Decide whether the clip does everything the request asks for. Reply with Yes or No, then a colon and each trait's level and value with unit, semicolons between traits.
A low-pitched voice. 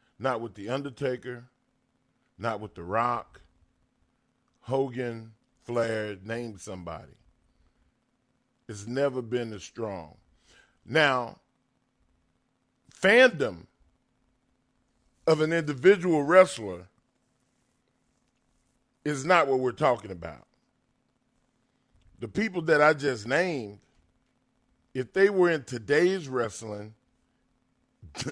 Yes: low, 125 Hz